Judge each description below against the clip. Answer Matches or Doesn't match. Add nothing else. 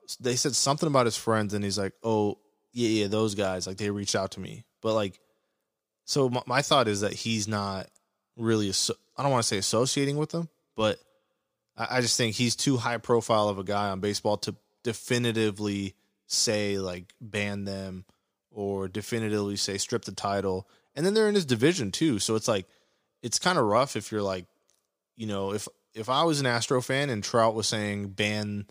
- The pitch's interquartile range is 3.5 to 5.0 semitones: Doesn't match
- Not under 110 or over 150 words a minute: Doesn't match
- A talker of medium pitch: Doesn't match